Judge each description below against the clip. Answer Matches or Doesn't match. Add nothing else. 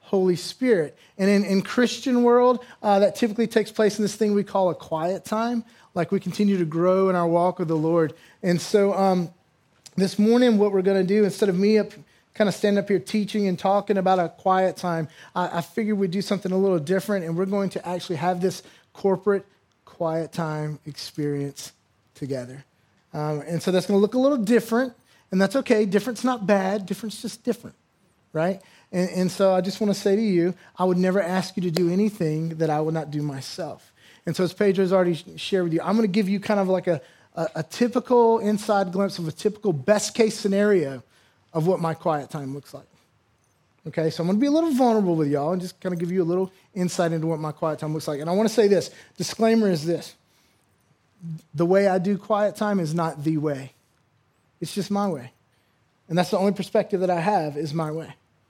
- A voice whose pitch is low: Doesn't match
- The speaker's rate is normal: Doesn't match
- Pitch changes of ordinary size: Matches